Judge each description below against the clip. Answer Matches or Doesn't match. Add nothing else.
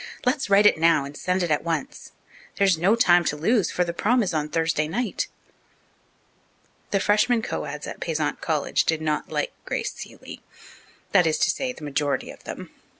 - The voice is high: Doesn't match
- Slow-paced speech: Doesn't match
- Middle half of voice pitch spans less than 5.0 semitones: Doesn't match